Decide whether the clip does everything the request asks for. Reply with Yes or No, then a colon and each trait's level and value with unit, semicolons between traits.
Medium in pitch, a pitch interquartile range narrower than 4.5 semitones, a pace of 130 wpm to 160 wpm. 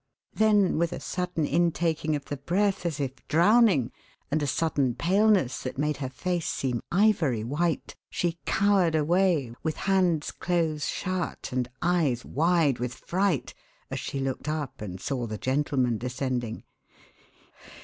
No: medium, 155 Hz; average, 5.2 semitones; average, 145 wpm